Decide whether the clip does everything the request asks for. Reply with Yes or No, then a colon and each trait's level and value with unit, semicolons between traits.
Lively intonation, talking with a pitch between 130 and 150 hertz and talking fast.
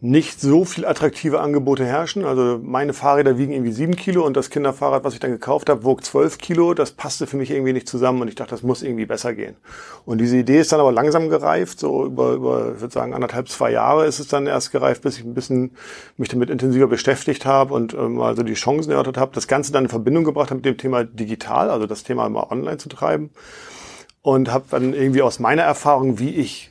No: average, 2.7 semitones; low, 135 Hz; fast, 235 wpm